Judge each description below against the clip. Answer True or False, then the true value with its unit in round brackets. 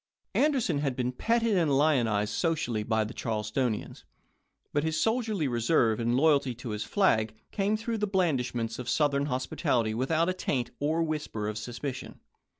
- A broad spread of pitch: True (6.1 semitones)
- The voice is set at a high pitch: False (135 Hz)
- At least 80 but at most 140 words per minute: False (160 wpm)